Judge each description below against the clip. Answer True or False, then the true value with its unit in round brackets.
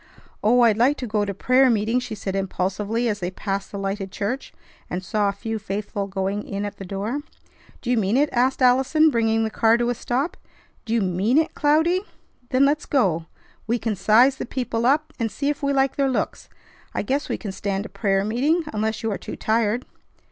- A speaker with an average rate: False (215 wpm)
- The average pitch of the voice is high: True (225 Hz)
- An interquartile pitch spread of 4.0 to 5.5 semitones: True (4.3 semitones)